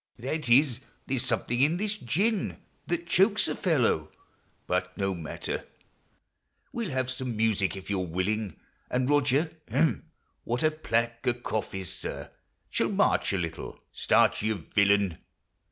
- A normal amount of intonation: No, wide, 7.0 semitones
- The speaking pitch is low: Yes, low, 120 Hz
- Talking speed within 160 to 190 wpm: Yes, average, 165 wpm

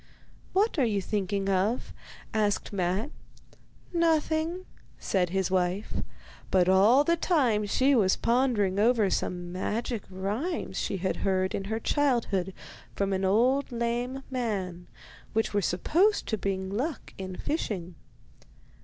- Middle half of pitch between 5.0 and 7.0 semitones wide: Yes, average, 5.3 semitones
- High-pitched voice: Yes, high, 210 Hz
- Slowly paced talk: Yes, slow, 130 wpm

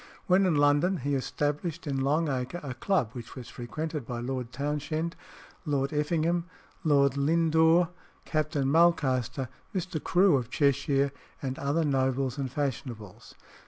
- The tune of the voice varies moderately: Yes, average, 3.4 semitones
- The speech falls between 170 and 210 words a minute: No, slow, 135 wpm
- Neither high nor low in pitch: Yes, medium, 145 Hz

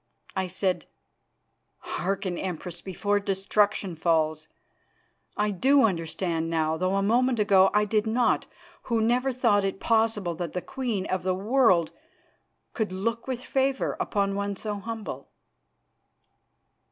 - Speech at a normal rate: No, slow, 130 wpm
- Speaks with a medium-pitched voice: No, high, 200 Hz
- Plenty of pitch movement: No, average, 3.6 semitones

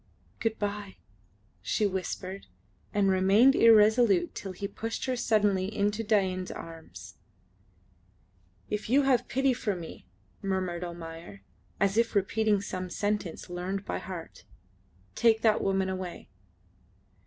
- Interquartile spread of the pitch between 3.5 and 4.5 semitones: No, average, 2.9 semitones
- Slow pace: Yes, slow, 120 wpm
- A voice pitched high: Yes, high, 200 Hz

